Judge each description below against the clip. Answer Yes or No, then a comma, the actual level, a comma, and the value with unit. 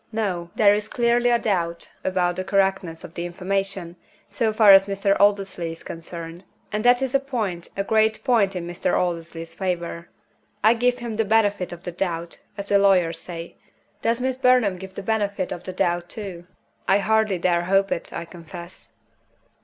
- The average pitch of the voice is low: No, high, 195 Hz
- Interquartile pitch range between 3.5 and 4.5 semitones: Yes, average, 3.8 semitones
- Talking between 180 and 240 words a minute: Yes, average, 185 wpm